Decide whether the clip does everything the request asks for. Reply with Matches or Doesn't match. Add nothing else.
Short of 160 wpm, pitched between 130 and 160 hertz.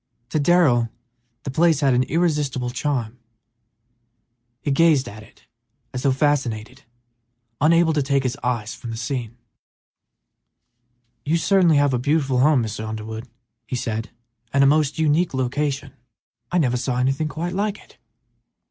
Matches